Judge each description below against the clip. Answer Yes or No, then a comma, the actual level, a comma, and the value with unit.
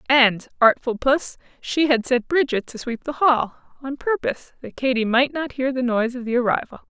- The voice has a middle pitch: No, very high, 255 Hz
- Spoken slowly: No, average, 200 wpm